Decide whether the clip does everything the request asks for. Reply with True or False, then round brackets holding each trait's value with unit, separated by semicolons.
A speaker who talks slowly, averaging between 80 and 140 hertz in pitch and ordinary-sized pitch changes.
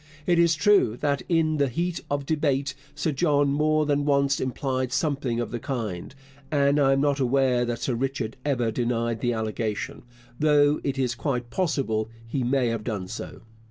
False (180 wpm; 135 Hz; 3.5 semitones)